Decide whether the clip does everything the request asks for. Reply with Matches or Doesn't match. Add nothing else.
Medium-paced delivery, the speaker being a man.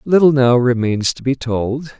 Matches